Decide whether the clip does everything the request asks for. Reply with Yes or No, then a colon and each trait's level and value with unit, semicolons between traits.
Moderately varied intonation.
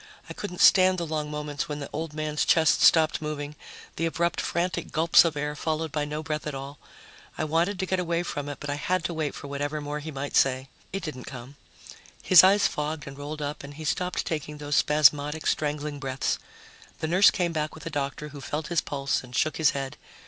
No: narrow, 2.1 semitones